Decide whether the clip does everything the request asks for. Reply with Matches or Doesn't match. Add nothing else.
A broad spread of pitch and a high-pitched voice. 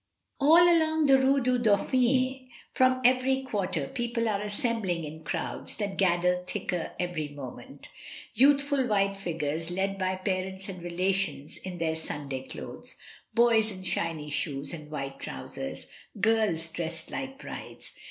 Matches